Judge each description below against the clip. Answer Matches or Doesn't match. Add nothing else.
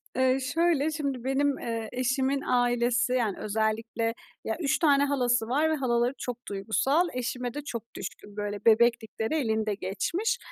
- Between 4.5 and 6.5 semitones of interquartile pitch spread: Doesn't match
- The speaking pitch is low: Doesn't match